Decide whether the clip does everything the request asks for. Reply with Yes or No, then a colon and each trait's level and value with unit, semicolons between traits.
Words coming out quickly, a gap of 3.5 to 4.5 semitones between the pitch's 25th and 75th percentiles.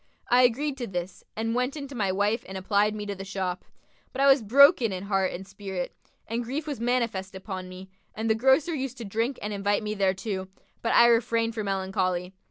Yes: fast, 215 wpm; average, 4.1 semitones